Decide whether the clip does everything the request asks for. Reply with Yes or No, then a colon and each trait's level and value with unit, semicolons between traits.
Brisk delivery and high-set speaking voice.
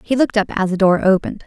Yes: fast, 285 wpm; high, 200 Hz